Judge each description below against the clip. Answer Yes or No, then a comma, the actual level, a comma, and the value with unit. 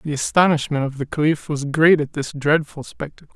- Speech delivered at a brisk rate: No, average, 195 wpm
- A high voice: No, medium, 150 Hz